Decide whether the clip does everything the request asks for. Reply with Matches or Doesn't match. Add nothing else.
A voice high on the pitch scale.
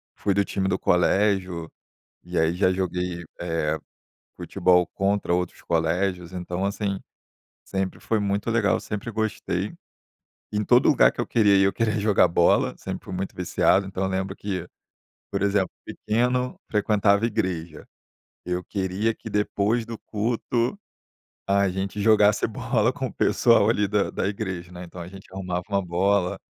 Doesn't match